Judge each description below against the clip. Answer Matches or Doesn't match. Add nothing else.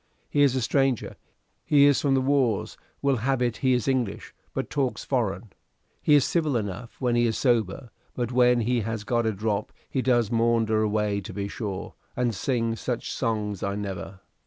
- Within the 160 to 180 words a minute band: Doesn't match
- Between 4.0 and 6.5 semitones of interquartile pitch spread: Doesn't match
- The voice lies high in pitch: Doesn't match